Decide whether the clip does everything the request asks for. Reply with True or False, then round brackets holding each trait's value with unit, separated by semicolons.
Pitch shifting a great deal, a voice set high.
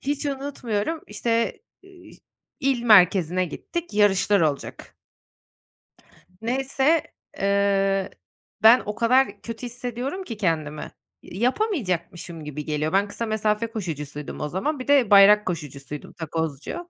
True (6.5 semitones; 210 Hz)